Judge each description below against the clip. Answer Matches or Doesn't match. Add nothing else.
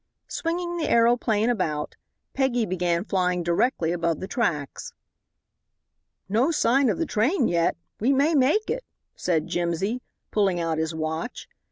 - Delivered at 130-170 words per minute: Matches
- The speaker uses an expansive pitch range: Matches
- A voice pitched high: Matches